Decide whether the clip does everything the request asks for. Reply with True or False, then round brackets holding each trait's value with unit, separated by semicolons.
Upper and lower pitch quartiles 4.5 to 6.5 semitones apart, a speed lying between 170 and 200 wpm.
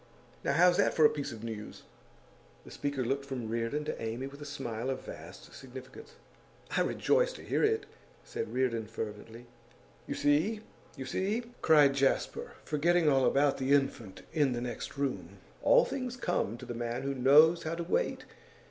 True (4.9 semitones; 175 wpm)